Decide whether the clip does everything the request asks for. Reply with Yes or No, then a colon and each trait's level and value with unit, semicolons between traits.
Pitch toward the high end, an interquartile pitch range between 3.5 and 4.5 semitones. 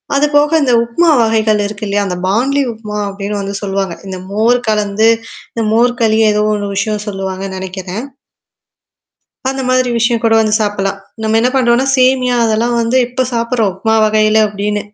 No: high, 220 Hz; average, 3.1 semitones